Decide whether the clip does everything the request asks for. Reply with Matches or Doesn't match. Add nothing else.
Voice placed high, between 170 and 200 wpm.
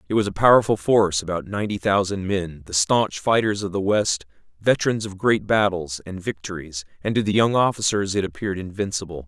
Doesn't match